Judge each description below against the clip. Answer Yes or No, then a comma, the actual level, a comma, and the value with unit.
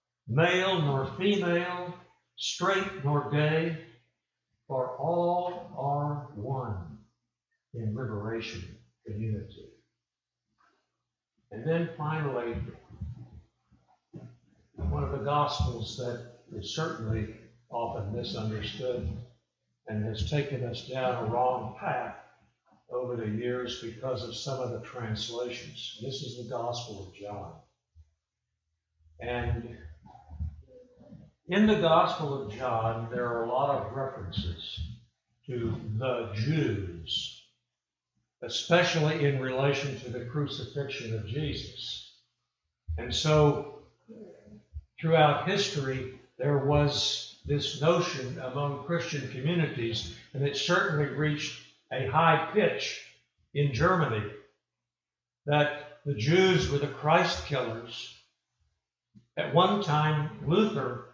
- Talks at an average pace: No, slow, 100 wpm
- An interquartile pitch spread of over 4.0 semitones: Yes, average, 4.9 semitones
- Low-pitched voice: Yes, low, 130 Hz